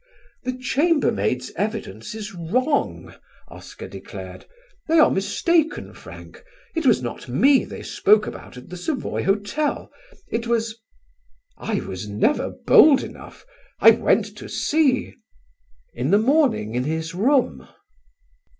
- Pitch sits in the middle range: No, high, 220 Hz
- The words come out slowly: Yes, slow, 125 wpm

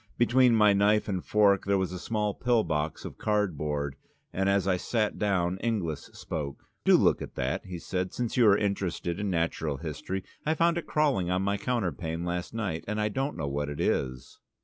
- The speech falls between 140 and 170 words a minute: No, average, 200 wpm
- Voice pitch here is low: Yes, very low, 95 Hz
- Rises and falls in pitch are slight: No, average, 4.3 semitones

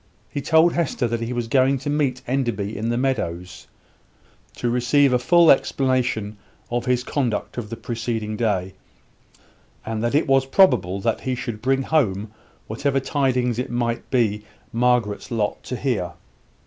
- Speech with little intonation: No, average, 3.4 semitones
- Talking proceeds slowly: No, average, 160 wpm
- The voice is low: Yes, low, 120 Hz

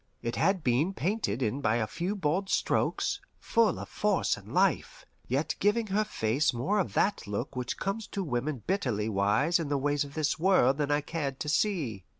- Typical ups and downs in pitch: No, wide, 7.6 semitones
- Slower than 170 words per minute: No, average, 195 wpm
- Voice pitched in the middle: Yes, medium, 150 Hz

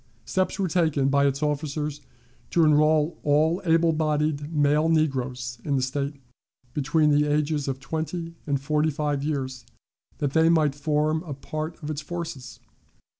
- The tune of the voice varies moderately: No, narrow, 2.0 semitones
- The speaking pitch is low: No, medium, 150 Hz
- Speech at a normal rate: Yes, average, 155 wpm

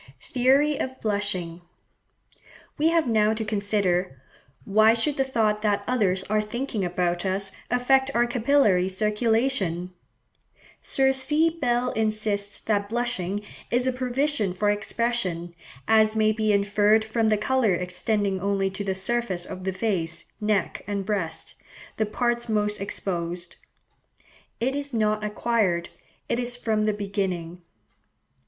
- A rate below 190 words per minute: Yes, slow, 135 wpm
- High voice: Yes, high, 215 Hz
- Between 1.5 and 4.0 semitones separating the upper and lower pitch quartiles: Yes, average, 3.7 semitones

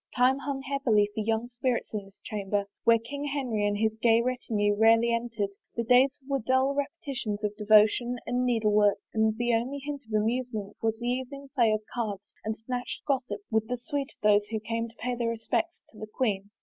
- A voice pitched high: Yes, high, 230 Hz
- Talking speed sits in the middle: No, fast, 210 wpm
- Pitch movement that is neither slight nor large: Yes, average, 3.0 semitones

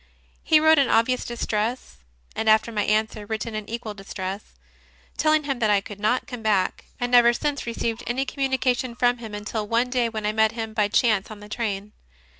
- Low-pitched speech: No, high, 225 Hz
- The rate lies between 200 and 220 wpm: Yes, fast, 205 wpm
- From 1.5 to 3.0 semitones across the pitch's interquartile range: Yes, narrow, 2.6 semitones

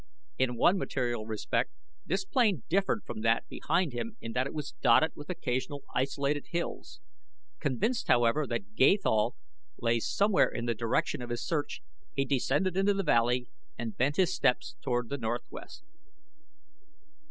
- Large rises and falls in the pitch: Yes, wide, 6.4 semitones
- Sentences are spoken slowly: No, average, 155 wpm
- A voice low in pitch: Yes, low, 130 Hz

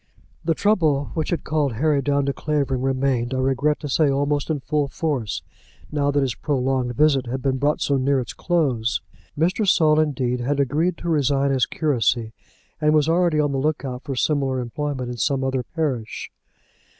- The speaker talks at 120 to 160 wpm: No, average, 185 wpm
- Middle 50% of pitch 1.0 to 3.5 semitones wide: Yes, average, 2.7 semitones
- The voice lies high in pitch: No, medium, 140 Hz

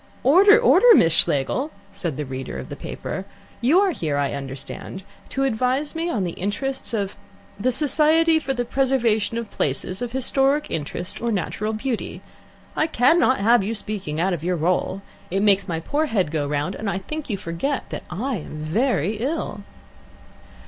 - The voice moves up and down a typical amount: No, wide, 7.5 semitones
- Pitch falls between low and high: No, high, 220 Hz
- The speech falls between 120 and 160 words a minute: No, average, 175 wpm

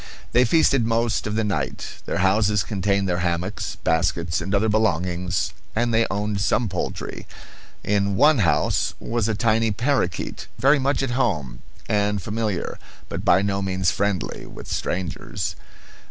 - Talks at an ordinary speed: Yes, average, 150 wpm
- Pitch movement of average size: Yes, average, 3.6 semitones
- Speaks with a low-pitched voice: Yes, low, 100 Hz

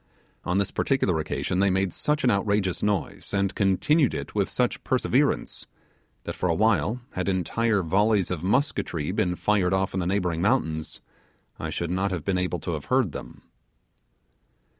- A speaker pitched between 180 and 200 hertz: No, very low, 95 Hz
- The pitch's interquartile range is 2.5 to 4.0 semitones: Yes, average, 2.8 semitones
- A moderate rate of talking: Yes, average, 165 wpm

